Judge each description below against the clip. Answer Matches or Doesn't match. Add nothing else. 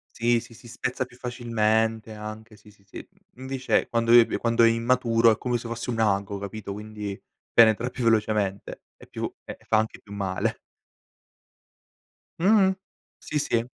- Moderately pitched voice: Doesn't match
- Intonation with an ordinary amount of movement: Doesn't match